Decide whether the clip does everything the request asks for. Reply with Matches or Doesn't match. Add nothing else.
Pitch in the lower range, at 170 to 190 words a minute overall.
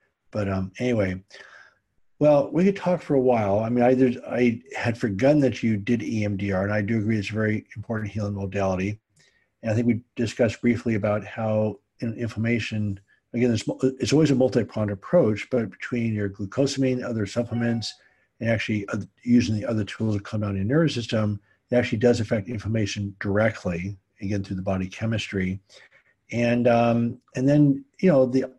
Matches